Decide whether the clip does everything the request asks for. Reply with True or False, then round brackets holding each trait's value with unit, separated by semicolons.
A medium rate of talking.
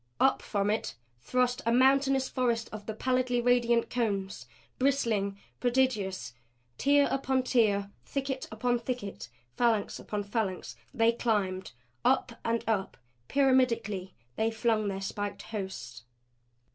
False (120 wpm)